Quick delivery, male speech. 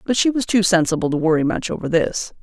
No: fast, 245 wpm; female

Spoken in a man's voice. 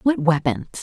No: female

